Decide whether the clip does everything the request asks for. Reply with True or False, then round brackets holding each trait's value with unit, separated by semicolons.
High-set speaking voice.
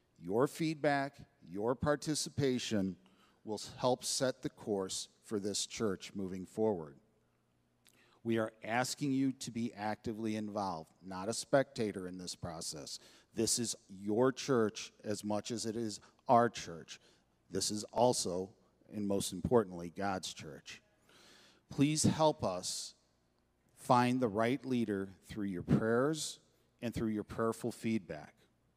False (110 Hz)